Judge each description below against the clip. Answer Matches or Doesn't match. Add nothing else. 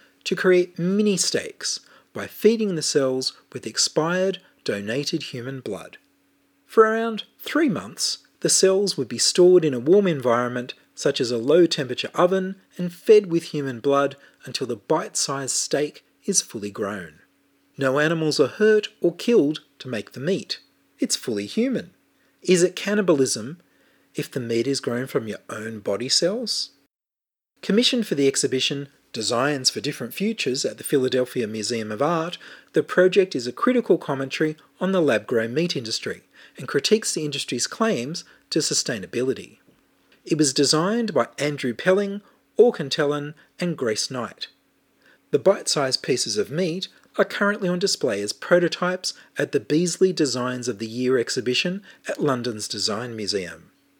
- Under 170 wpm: Matches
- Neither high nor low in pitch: Matches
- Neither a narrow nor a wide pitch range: Doesn't match